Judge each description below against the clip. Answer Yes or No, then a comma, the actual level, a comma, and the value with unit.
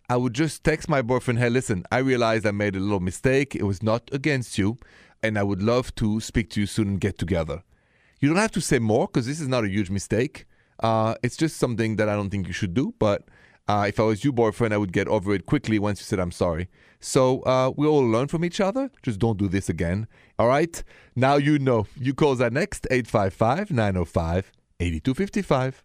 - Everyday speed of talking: No, fast, 230 wpm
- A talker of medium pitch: No, low, 115 Hz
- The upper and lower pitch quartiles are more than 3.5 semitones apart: Yes, average, 4.8 semitones